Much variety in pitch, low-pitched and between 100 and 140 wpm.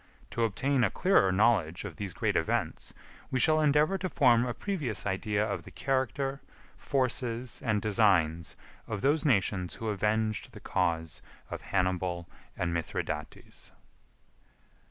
Yes: wide, 6.1 semitones; low, 110 Hz; slow, 135 wpm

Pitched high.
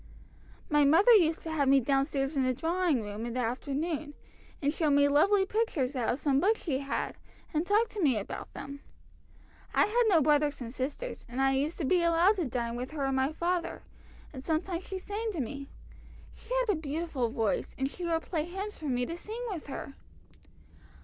Yes: very high, 300 Hz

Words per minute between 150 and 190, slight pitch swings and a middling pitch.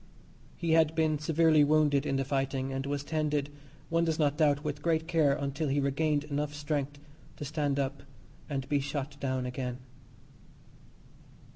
Yes: average, 160 wpm; narrow, 1.9 semitones; medium, 145 Hz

